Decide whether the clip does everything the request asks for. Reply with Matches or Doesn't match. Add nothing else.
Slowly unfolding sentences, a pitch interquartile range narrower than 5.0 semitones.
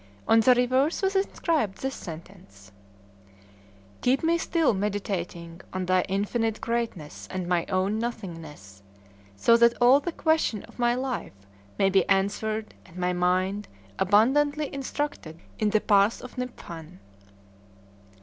Doesn't match